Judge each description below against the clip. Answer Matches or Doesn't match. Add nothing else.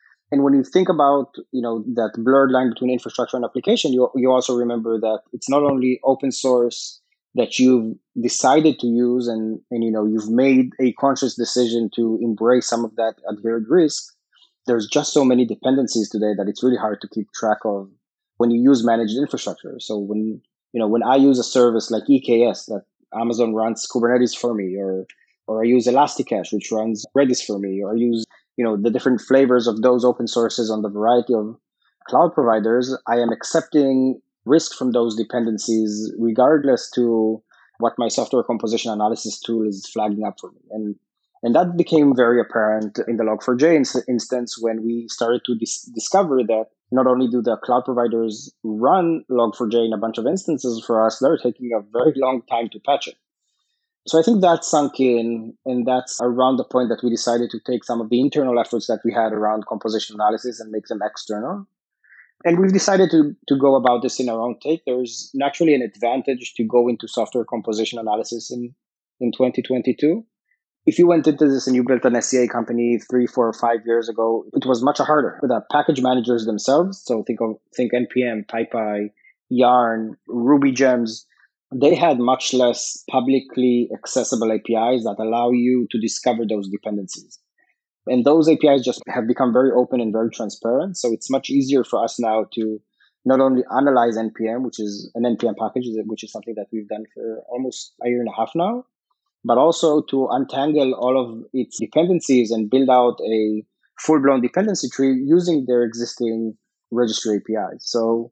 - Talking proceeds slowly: Doesn't match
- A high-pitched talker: Doesn't match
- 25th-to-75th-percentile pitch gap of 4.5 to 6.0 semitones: Doesn't match